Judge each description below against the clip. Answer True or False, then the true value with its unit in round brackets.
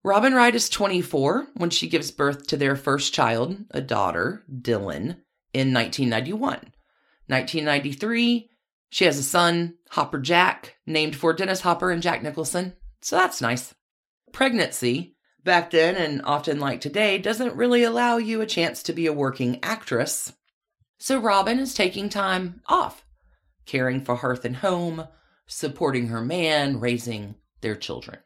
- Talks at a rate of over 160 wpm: False (145 wpm)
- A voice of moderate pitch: True (160 Hz)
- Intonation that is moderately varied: False (6.7 semitones)